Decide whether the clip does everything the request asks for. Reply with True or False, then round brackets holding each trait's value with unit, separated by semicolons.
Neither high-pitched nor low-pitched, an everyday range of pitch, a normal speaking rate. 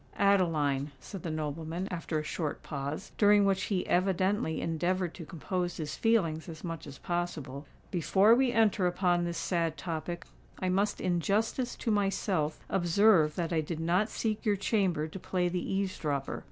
True (175 Hz; 3.6 semitones; 170 wpm)